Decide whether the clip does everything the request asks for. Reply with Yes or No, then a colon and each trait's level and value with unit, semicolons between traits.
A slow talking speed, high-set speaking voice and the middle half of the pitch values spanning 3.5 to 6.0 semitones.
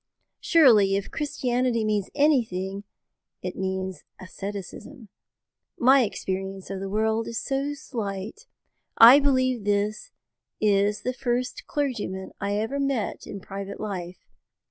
Yes: slow, 120 wpm; high, 215 Hz; average, 4.7 semitones